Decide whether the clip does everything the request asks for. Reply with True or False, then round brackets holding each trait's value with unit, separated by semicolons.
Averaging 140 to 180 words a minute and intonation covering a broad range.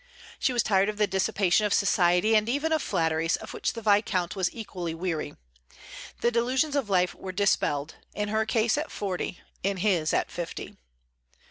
False (175 wpm; 3.7 semitones)